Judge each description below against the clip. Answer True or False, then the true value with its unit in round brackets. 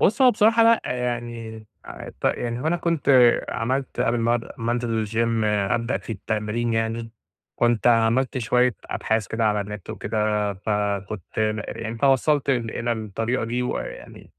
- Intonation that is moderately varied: False (2.2 semitones)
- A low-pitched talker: True (115 Hz)